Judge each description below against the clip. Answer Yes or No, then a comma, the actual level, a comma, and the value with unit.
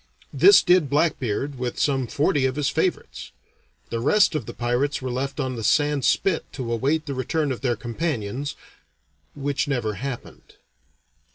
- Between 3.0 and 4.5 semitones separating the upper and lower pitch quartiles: Yes, average, 3.3 semitones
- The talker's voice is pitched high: No, low, 135 Hz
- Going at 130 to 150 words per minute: No, average, 160 wpm